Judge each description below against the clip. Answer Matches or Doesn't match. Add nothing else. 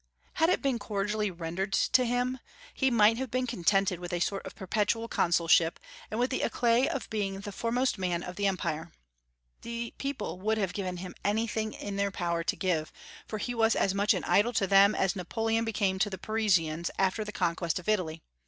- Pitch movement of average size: Matches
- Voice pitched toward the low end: Doesn't match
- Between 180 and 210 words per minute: Matches